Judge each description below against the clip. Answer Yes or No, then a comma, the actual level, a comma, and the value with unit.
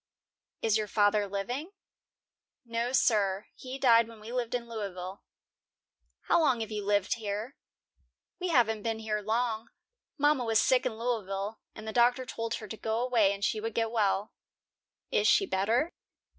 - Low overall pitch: No, high, 225 Hz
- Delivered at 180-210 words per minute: No, average, 165 wpm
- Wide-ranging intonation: No, average, 2.8 semitones